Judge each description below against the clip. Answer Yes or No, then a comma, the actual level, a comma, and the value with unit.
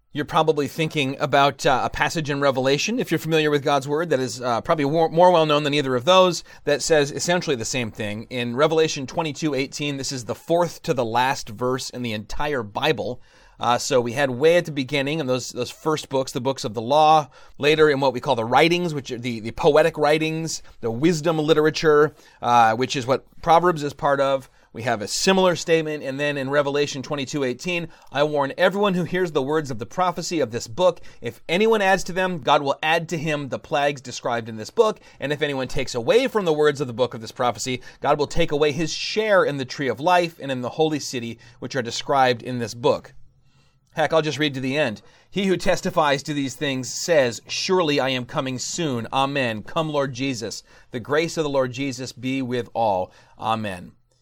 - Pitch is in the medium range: Yes, medium, 145 Hz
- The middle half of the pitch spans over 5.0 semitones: No, average, 3.8 semitones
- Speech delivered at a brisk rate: Yes, fast, 220 wpm